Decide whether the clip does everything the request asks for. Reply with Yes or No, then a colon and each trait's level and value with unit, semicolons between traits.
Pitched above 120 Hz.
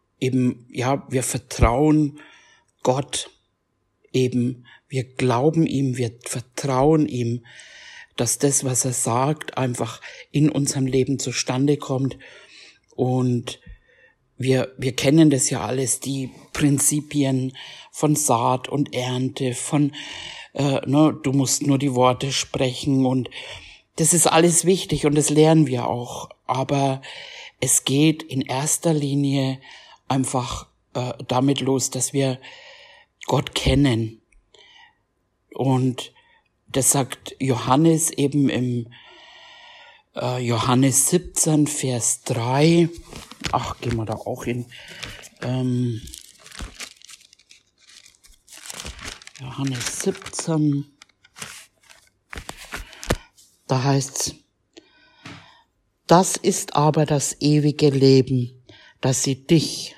Yes: low, 135 Hz